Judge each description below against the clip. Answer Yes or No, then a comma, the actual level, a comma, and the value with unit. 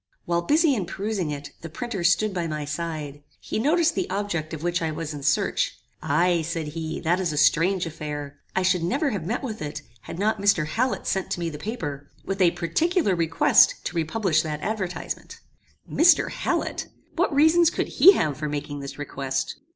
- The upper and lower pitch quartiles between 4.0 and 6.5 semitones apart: Yes, average, 5.3 semitones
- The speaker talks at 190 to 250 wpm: Yes, average, 195 wpm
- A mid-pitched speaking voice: Yes, medium, 170 Hz